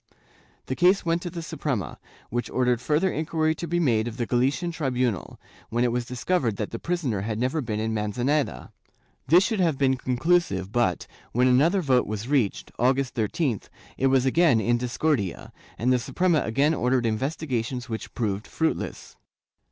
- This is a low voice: Yes, low, 125 Hz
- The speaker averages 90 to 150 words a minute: No, average, 170 wpm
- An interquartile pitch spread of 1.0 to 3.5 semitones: No, wide, 5.4 semitones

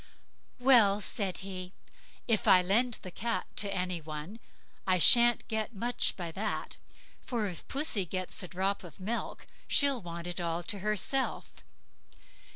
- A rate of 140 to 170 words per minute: Yes, average, 145 wpm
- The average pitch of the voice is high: Yes, high, 195 Hz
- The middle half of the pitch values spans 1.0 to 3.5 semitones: No, average, 4.2 semitones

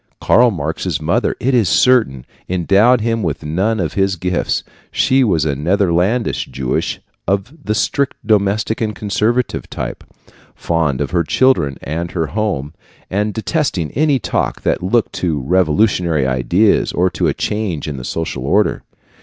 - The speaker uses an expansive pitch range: Yes, wide, 5.7 semitones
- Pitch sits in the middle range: No, very low, 95 Hz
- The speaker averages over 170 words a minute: No, average, 155 wpm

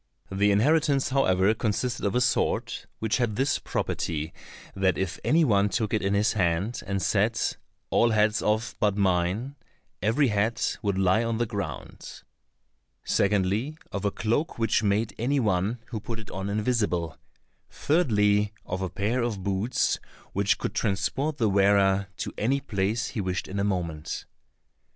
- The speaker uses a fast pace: No, average, 160 wpm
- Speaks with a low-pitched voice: Yes, low, 105 Hz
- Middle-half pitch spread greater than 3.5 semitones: No, average, 3.2 semitones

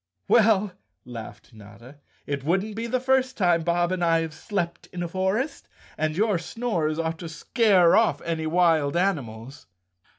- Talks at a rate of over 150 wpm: Yes, average, 160 wpm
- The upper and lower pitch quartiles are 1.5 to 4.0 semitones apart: No, average, 4.7 semitones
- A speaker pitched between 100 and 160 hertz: No, medium, 175 Hz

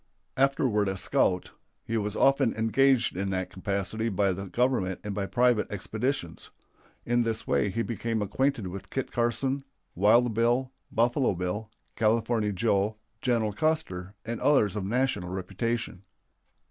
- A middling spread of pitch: Yes, average, 3.8 semitones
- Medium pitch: No, low, 110 Hz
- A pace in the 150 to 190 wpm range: No, average, 140 wpm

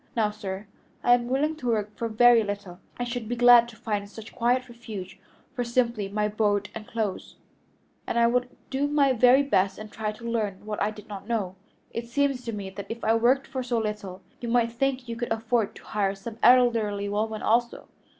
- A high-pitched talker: Yes, high, 230 Hz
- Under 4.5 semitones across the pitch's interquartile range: Yes, narrow, 2.6 semitones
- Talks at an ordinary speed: No, fast, 215 wpm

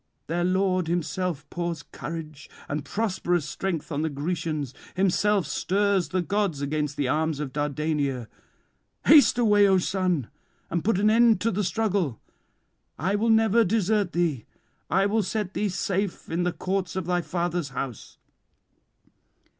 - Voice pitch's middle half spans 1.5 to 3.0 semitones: No, average, 4.6 semitones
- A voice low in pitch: No, medium, 175 Hz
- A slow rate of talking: No, average, 145 wpm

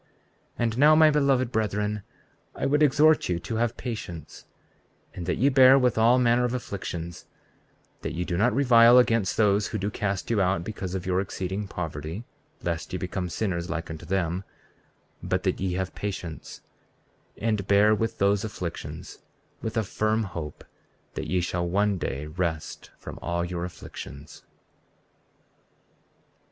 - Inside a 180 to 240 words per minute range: No, average, 160 wpm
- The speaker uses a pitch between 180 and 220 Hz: No, low, 100 Hz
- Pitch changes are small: No, average, 4.7 semitones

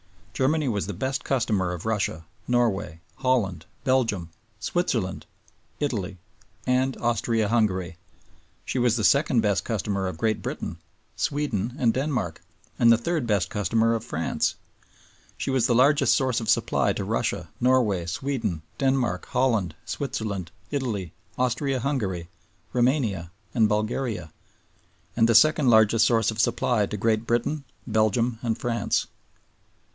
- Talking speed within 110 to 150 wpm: Yes, slow, 135 wpm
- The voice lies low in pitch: Yes, low, 115 Hz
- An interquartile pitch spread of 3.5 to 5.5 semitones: Yes, average, 4.1 semitones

